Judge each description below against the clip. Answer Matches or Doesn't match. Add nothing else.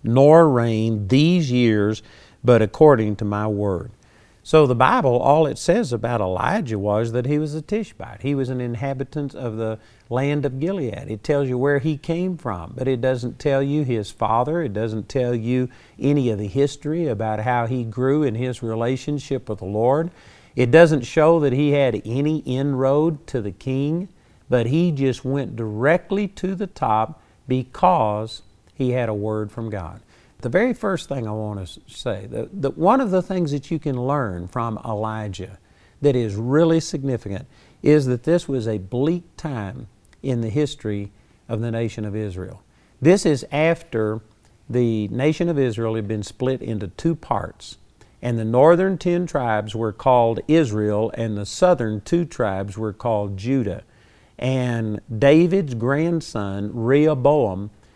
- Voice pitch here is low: Matches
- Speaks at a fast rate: Doesn't match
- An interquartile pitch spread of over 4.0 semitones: Matches